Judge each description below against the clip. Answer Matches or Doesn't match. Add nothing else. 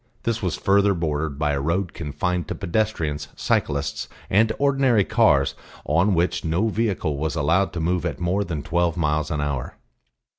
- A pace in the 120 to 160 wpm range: Doesn't match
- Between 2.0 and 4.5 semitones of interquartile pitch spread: Doesn't match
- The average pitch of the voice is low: Matches